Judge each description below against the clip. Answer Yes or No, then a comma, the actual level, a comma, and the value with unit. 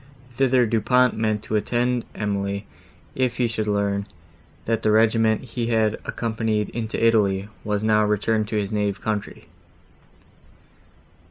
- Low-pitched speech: Yes, low, 110 Hz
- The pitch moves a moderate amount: No, narrow, 1.7 semitones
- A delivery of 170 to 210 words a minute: No, slow, 135 wpm